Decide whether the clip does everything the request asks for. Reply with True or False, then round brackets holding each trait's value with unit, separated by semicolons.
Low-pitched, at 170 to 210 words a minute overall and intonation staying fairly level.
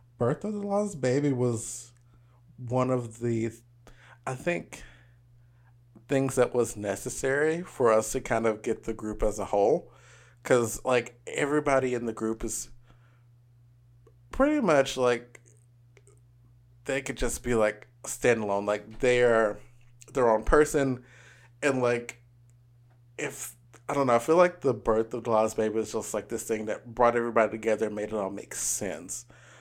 False (120 Hz; 155 wpm; 2.0 semitones)